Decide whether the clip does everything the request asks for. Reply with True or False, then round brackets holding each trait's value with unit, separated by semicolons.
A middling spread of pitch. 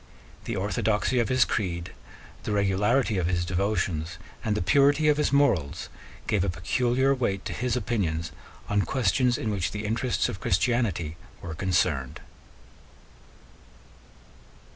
False (5.7 semitones)